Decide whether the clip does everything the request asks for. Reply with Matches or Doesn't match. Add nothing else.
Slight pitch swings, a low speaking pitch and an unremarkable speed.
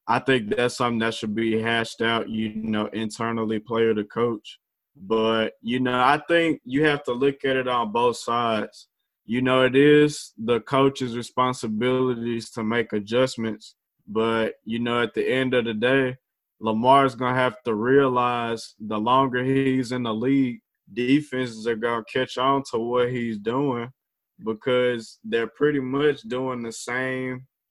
Matches